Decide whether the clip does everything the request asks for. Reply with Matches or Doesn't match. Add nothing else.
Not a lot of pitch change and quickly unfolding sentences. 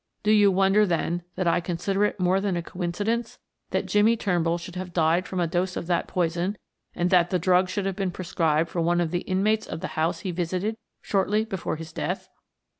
Matches